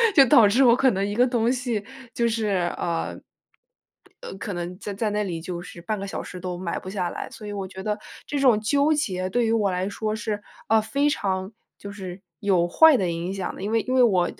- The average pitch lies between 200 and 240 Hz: Yes, high, 205 Hz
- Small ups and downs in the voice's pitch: No, average, 3.9 semitones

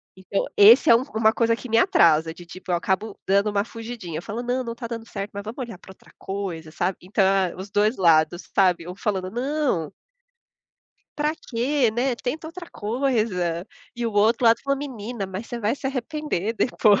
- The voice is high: Yes, high, 215 Hz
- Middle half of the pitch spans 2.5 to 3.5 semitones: No, average, 4.3 semitones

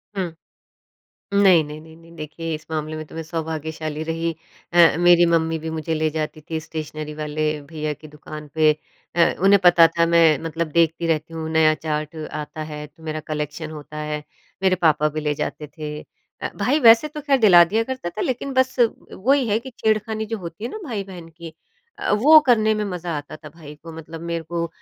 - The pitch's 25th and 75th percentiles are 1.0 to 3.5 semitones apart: Yes, average, 2.9 semitones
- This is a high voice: No, medium, 165 Hz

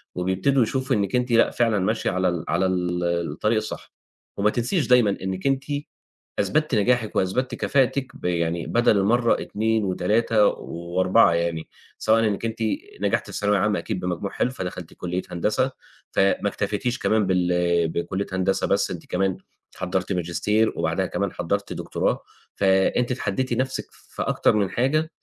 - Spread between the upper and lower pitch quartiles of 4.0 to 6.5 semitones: Yes, average, 4.5 semitones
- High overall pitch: No, low, 100 Hz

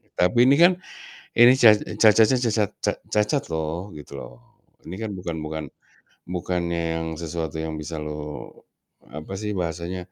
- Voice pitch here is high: No, very low, 85 Hz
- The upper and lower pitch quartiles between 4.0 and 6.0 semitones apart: Yes, average, 5.0 semitones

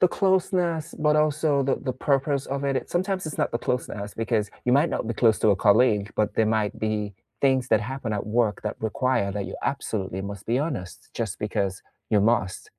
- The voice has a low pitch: Yes, low, 120 Hz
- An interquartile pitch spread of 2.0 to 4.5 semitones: No, average, 5.0 semitones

